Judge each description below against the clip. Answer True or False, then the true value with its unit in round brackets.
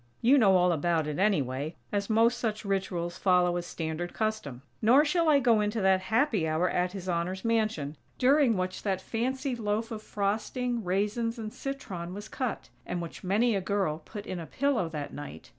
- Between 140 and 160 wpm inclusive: False (190 wpm)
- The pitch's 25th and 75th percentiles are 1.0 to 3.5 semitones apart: False (4.6 semitones)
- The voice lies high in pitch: True (200 Hz)